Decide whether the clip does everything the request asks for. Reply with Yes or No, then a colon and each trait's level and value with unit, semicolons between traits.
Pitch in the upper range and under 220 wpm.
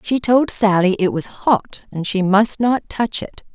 Yes: high, 210 Hz; fast, 205 wpm